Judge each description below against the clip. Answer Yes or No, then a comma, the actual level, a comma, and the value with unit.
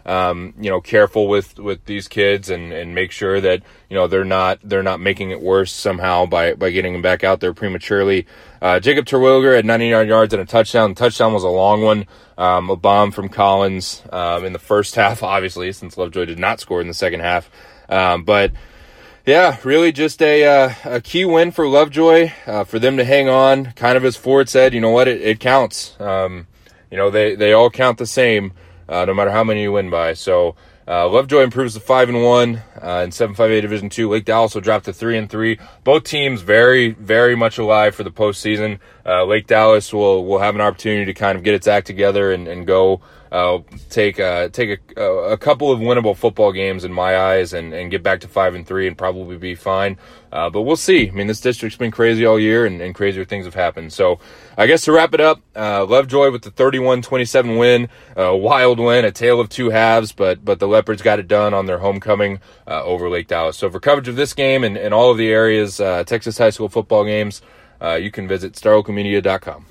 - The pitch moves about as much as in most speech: Yes, average, 4.0 semitones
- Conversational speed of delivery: No, fast, 230 wpm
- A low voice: Yes, low, 105 Hz